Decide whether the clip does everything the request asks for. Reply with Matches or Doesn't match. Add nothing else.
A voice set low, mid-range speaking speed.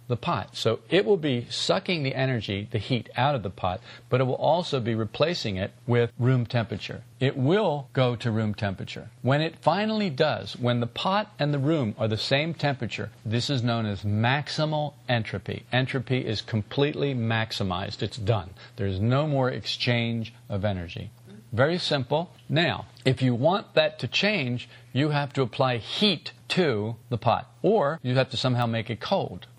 Matches